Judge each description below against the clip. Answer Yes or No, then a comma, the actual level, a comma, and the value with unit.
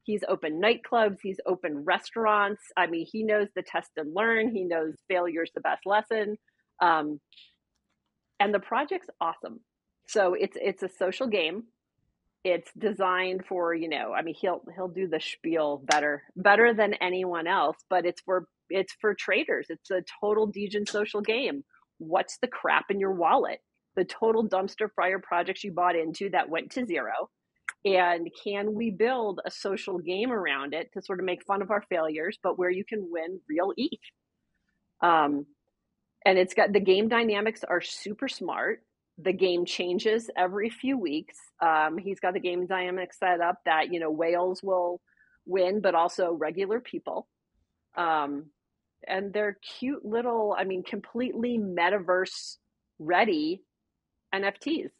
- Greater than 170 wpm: No, average, 160 wpm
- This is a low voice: No, high, 190 Hz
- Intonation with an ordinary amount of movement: Yes, average, 3.1 semitones